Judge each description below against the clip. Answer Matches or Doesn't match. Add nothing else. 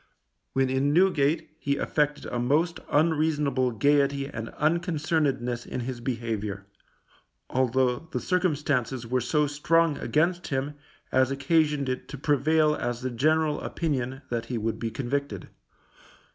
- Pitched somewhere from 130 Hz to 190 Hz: Matches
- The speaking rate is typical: Doesn't match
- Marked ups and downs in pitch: Doesn't match